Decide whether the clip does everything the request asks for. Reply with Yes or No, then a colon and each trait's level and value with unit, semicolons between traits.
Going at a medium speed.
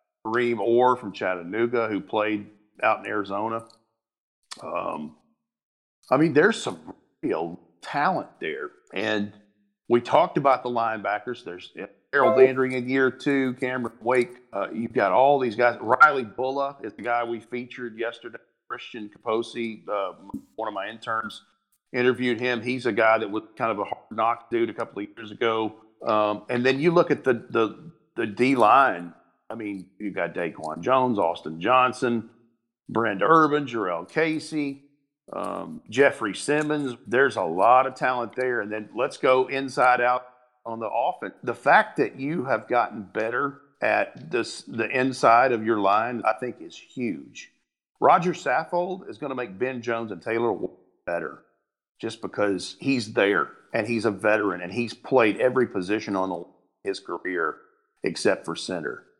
Yes: average, 160 wpm